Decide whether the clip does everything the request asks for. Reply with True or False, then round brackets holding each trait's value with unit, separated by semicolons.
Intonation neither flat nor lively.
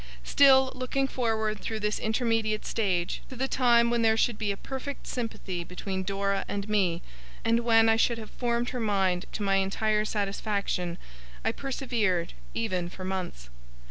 True (3.4 semitones)